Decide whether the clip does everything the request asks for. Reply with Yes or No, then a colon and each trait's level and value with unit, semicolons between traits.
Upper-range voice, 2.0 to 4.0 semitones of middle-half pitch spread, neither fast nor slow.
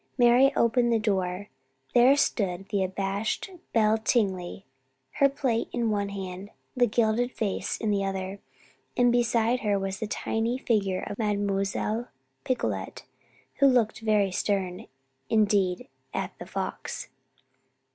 No: high, 210 Hz; average, 3.4 semitones; slow, 130 wpm